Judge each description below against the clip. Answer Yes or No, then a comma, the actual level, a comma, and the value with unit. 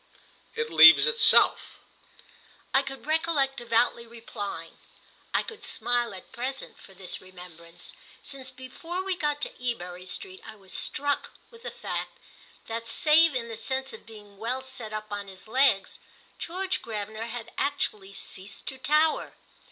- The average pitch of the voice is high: Yes, high, 240 Hz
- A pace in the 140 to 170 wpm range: Yes, average, 150 wpm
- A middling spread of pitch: No, wide, 5.7 semitones